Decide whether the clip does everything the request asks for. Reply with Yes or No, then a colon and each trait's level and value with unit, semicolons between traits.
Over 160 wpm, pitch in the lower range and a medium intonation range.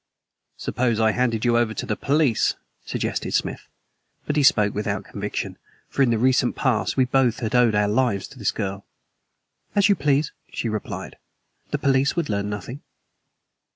Yes: average, 170 wpm; low, 120 Hz; average, 3.9 semitones